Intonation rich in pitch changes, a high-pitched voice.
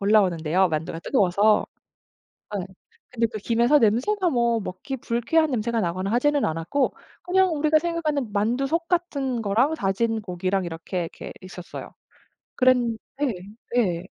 Yes: wide, 6.7 semitones; high, 230 Hz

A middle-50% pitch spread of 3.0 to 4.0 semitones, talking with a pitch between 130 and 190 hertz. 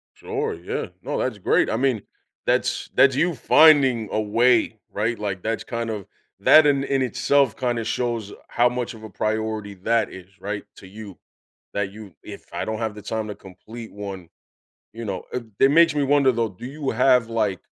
No: average, 3.5 semitones; low, 115 Hz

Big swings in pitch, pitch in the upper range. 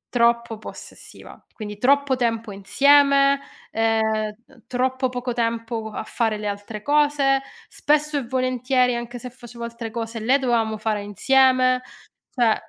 No: average, 2.7 semitones; high, 240 Hz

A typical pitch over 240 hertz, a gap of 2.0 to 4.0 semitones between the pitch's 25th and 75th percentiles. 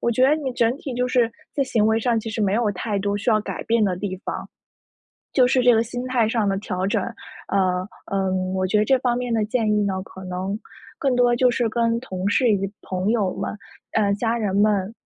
No: high, 220 Hz; average, 3.5 semitones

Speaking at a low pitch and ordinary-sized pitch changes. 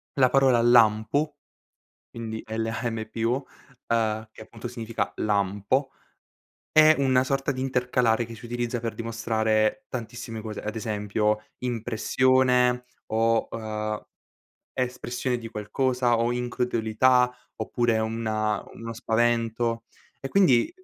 No: low, 115 Hz; narrow, 2.2 semitones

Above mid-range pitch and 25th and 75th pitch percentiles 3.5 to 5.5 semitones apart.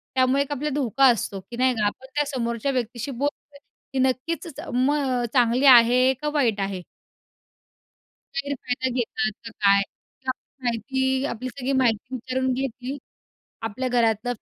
No: very high, 255 Hz; narrow, 2.6 semitones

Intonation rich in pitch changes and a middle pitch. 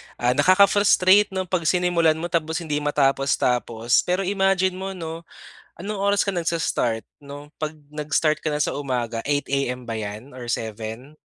Yes: wide, 6.1 semitones; medium, 150 Hz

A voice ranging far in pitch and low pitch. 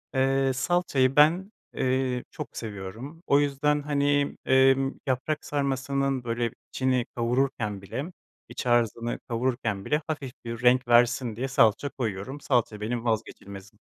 No: average, 2.9 semitones; low, 130 Hz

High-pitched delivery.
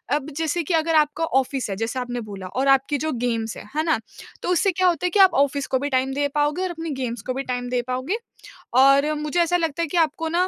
Yes: very high, 290 Hz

